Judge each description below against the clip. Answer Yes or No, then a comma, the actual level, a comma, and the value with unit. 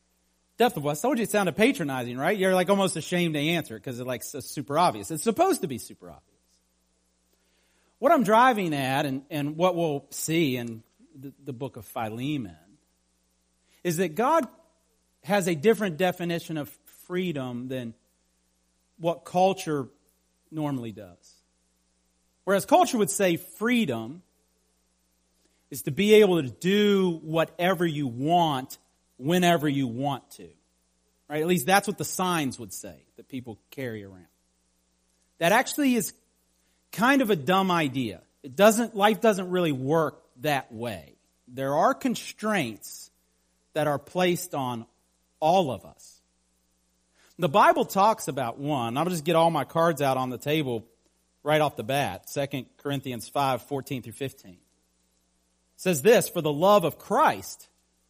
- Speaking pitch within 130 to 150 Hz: Yes, medium, 140 Hz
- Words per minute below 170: Yes, average, 150 wpm